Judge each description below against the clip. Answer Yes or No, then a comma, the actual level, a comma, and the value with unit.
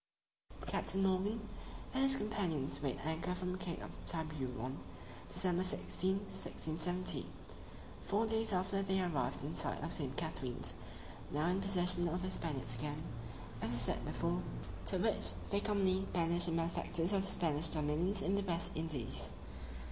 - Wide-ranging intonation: No, average, 3.7 semitones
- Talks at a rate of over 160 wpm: No, average, 155 wpm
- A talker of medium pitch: Yes, medium, 175 Hz